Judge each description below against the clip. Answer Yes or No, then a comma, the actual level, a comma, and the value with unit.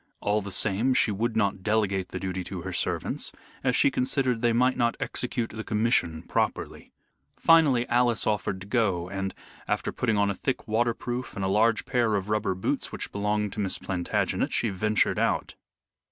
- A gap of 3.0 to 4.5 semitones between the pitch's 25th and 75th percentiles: Yes, average, 3.5 semitones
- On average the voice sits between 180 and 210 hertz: No, low, 105 Hz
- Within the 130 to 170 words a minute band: No, average, 180 wpm